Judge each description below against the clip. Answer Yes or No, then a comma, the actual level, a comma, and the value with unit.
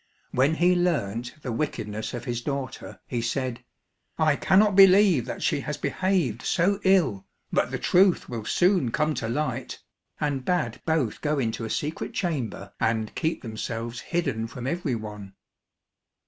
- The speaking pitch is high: No, low, 135 Hz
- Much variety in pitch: Yes, wide, 7.0 semitones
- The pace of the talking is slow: No, average, 155 wpm